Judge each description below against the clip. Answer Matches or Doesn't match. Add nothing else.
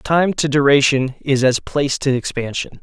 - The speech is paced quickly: Doesn't match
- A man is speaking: Matches